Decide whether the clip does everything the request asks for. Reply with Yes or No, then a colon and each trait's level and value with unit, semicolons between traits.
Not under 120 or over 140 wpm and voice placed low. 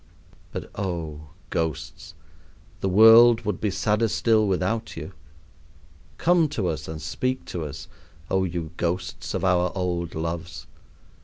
Yes: slow, 135 wpm; very low, 90 Hz